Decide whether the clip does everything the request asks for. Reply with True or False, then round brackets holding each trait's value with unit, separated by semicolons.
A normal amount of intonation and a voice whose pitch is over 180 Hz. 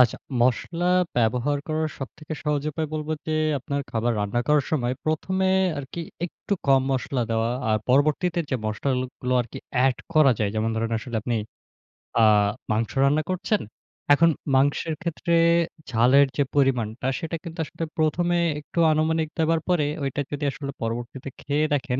False (4.2 semitones; 140 Hz)